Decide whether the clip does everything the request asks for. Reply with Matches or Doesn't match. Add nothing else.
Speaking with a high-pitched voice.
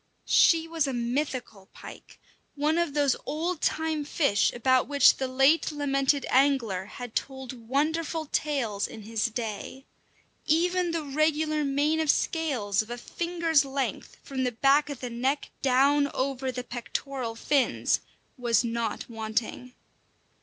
Matches